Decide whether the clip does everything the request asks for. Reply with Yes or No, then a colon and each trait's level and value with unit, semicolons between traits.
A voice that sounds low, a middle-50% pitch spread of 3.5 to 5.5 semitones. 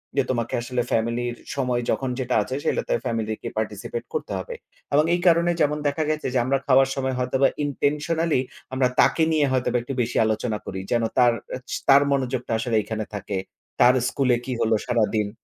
No: low, 125 Hz; average, 3.1 semitones